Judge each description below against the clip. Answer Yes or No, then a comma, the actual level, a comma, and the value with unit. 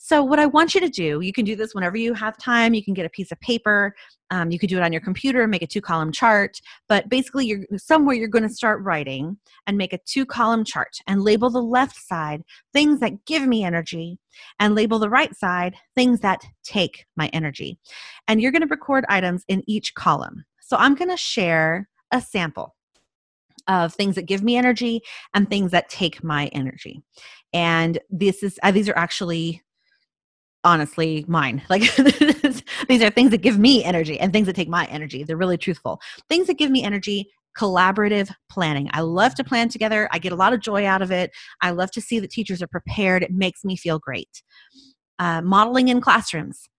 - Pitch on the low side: No, high, 200 Hz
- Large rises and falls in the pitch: Yes, wide, 5.7 semitones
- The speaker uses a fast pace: Yes, fast, 210 wpm